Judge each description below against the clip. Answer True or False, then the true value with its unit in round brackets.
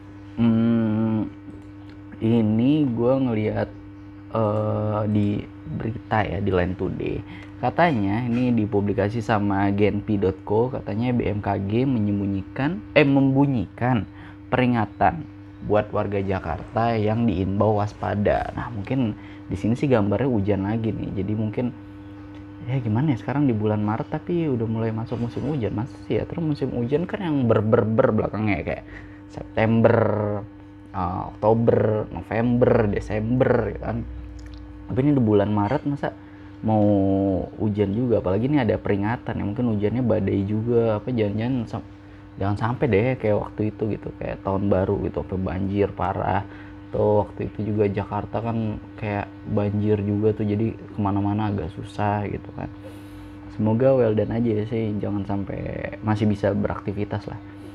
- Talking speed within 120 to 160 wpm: True (135 wpm)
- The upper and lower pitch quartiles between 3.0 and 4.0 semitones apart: False (2.4 semitones)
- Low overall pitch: True (105 Hz)